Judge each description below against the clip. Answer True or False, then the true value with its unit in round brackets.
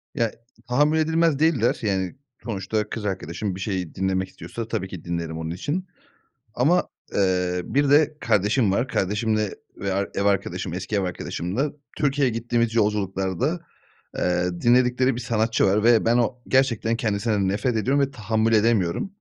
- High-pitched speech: False (110 Hz)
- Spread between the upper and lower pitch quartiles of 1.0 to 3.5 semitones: False (4.6 semitones)